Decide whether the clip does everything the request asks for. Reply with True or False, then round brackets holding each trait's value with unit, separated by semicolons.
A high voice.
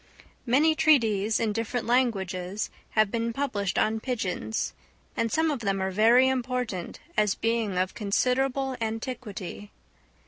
True (225 Hz)